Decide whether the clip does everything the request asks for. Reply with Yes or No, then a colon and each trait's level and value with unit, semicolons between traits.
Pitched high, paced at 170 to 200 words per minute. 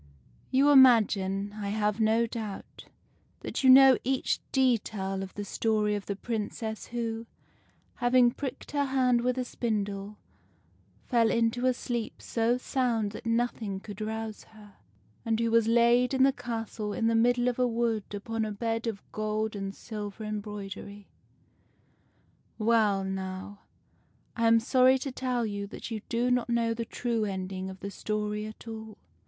No: high, 225 Hz; average, 160 wpm